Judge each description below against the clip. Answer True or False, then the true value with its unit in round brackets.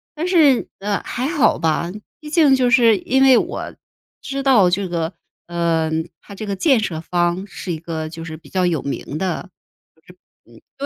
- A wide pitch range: True (7.9 semitones)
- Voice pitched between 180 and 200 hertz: True (190 Hz)